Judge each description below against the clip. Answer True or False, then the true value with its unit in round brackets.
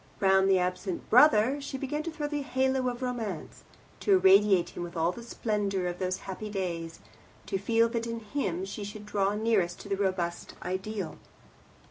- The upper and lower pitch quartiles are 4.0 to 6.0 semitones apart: True (4.4 semitones)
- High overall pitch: True (205 Hz)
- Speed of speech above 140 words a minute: True (180 wpm)